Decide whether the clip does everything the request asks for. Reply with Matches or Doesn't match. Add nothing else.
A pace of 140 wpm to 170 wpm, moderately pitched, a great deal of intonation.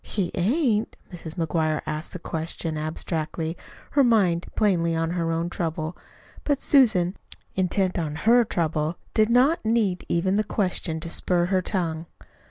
Doesn't match